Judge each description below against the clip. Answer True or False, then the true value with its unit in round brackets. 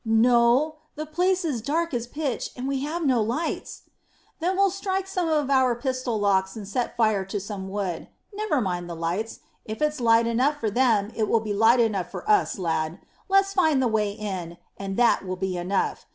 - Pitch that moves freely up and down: True (7.1 semitones)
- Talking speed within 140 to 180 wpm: False (200 wpm)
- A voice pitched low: False (235 Hz)